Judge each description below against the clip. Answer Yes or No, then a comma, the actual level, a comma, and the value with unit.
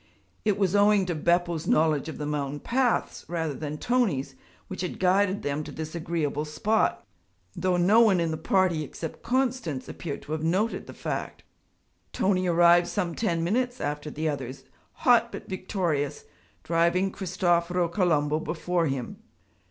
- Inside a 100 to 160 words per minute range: Yes, average, 155 wpm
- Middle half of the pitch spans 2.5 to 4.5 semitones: Yes, average, 3.8 semitones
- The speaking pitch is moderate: Yes, medium, 170 Hz